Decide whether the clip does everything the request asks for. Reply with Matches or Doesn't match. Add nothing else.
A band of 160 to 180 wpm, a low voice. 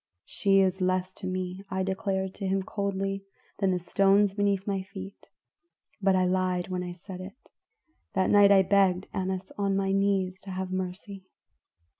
Doesn't match